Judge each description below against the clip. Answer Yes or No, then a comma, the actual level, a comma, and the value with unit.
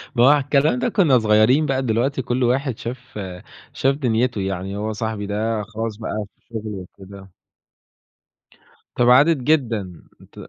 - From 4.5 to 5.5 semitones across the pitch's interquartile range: No, average, 3.7 semitones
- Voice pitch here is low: Yes, low, 115 Hz